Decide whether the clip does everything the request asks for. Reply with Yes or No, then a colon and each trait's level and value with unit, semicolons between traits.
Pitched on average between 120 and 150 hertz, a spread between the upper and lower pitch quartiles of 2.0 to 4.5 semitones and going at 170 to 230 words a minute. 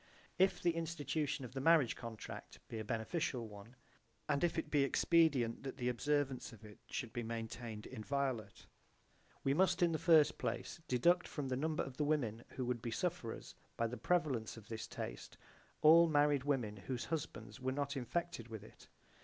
No: low, 135 Hz; average, 5.0 semitones; average, 180 wpm